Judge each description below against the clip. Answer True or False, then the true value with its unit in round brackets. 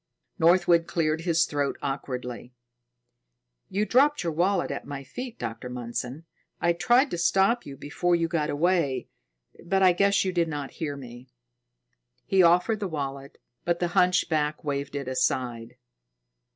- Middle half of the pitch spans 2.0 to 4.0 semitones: False (4.6 semitones)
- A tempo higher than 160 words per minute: False (150 wpm)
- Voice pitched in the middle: True (165 Hz)